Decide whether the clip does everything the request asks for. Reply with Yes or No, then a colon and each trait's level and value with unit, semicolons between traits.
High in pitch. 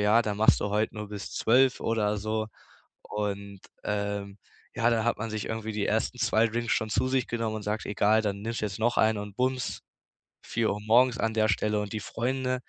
No: low, 110 Hz